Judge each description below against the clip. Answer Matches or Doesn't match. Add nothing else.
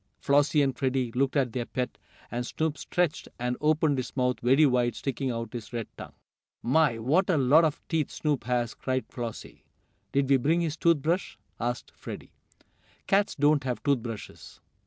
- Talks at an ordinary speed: Matches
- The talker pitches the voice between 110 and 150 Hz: Matches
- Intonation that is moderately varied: Matches